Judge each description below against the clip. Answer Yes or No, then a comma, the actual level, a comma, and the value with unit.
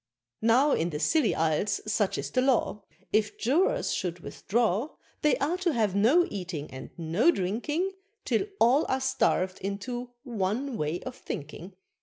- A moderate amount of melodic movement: No, wide, 6.2 semitones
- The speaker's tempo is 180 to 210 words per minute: No, average, 155 wpm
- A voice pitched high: Yes, high, 225 Hz